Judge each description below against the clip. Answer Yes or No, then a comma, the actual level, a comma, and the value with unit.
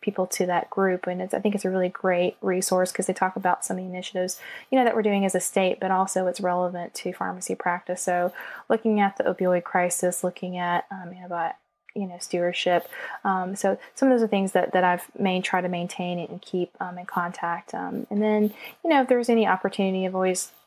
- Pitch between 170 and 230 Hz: Yes, medium, 185 Hz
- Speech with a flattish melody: Yes, narrow, 1.8 semitones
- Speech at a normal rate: No, fast, 235 wpm